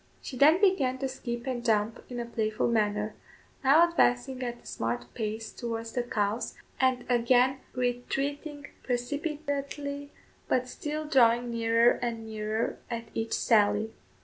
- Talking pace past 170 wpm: No, average, 140 wpm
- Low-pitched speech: No, high, 245 Hz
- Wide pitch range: No, average, 3.2 semitones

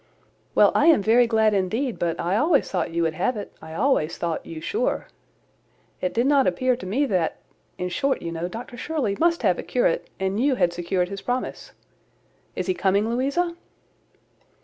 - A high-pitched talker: Yes, high, 215 Hz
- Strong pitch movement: Yes, wide, 7.0 semitones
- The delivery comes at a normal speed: Yes, average, 185 wpm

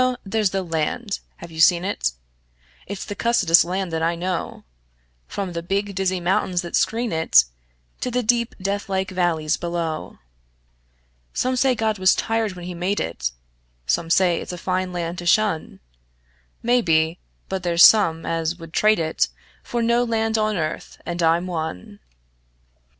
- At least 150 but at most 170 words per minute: Yes, average, 160 wpm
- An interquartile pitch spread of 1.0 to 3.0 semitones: No, average, 3.8 semitones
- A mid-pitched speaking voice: Yes, medium, 180 Hz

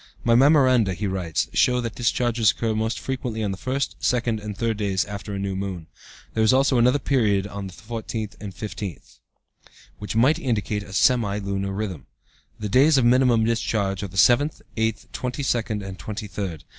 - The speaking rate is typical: Yes, average, 180 wpm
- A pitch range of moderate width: Yes, average, 3.5 semitones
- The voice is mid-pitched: No, low, 110 Hz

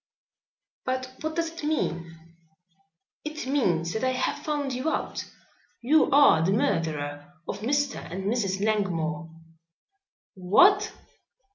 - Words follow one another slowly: Yes, slow, 120 wpm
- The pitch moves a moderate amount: No, wide, 8.9 semitones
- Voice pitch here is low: No, high, 235 Hz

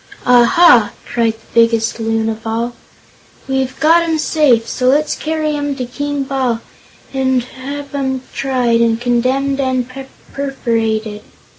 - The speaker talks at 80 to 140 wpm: Yes, slow, 135 wpm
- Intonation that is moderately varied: Yes, average, 3.2 semitones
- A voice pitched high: Yes, very high, 255 Hz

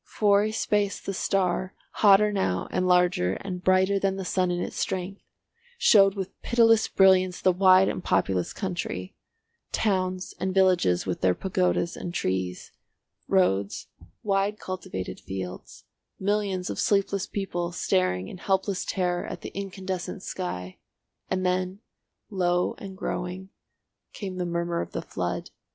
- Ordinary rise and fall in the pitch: No, narrow, 1.9 semitones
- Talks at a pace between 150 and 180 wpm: No, average, 140 wpm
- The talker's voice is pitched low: No, medium, 185 Hz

